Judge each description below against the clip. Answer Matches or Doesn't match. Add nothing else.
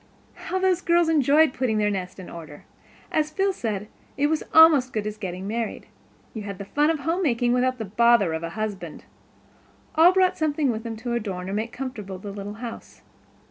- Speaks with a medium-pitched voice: Doesn't match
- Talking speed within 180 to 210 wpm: Matches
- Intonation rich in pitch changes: Matches